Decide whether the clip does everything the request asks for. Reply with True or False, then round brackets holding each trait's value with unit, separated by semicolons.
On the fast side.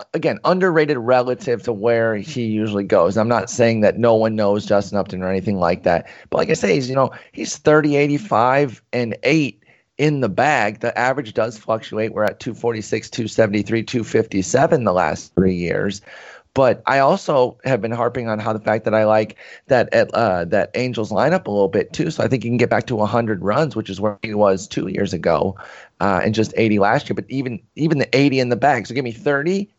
True (220 wpm)